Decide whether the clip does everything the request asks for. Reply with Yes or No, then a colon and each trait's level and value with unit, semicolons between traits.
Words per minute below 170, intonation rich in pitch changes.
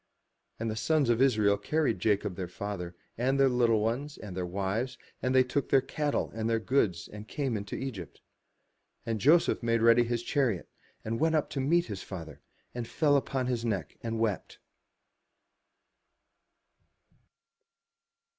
No: average, 160 wpm; average, 4.5 semitones